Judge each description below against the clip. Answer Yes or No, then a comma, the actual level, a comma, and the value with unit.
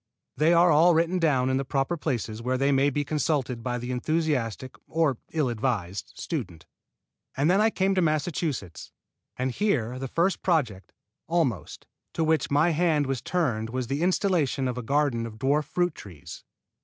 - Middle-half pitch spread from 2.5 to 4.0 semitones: No, average, 4.8 semitones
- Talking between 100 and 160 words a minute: No, average, 175 wpm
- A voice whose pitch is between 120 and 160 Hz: Yes, medium, 140 Hz